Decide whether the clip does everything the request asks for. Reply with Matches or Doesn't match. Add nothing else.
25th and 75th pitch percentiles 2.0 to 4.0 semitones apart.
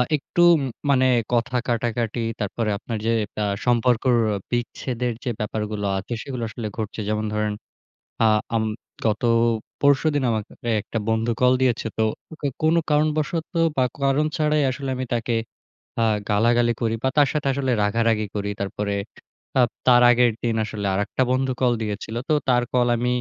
Matches